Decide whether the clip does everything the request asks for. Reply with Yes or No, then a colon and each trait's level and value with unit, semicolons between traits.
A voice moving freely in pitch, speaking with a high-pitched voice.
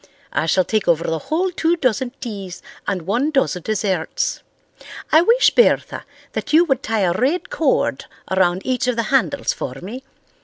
Yes: wide, 7.9 semitones; high, 230 Hz